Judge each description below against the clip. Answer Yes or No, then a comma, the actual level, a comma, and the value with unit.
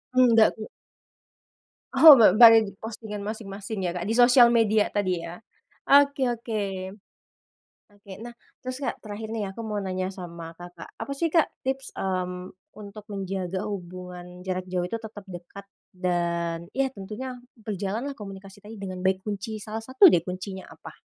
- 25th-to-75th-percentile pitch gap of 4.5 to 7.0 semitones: No, average, 3.6 semitones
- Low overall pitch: No, high, 200 Hz